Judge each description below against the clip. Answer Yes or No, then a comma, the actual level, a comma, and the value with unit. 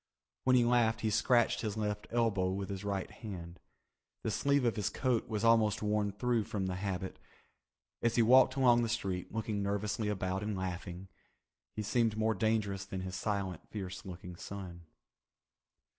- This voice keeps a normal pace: Yes, average, 170 wpm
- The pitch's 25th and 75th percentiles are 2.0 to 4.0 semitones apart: Yes, average, 3.1 semitones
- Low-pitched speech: Yes, low, 105 Hz